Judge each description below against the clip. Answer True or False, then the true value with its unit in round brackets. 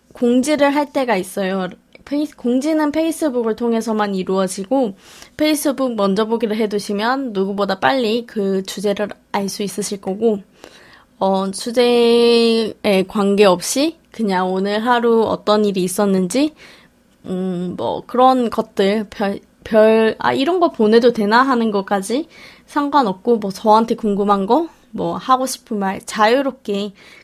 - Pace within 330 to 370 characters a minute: False (275 characters per minute)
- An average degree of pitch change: True (3.8 semitones)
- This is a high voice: True (220 Hz)